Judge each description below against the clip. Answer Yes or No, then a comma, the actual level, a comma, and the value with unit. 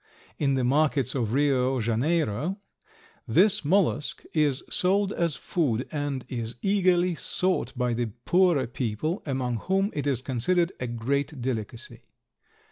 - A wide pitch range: Yes, wide, 5.9 semitones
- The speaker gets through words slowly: Yes, slow, 130 wpm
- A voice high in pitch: No, medium, 140 Hz